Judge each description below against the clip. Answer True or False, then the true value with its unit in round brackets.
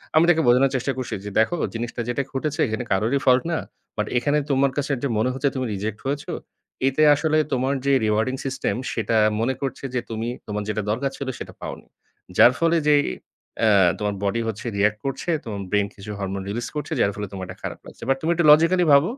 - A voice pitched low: True (125 Hz)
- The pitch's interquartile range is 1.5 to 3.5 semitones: False (4.7 semitones)